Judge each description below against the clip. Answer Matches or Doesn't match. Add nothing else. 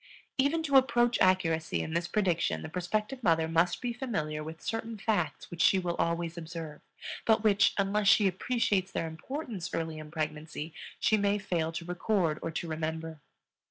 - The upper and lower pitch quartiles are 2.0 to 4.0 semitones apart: Doesn't match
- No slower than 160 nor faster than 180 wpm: Matches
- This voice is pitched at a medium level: Matches